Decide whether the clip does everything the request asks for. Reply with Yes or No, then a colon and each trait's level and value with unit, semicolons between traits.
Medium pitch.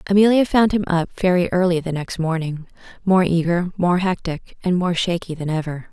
Yes: medium, 175 Hz